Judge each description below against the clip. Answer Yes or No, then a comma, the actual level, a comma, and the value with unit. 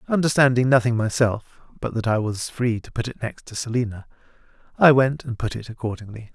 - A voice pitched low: Yes, low, 120 Hz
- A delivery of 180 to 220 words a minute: Yes, average, 190 wpm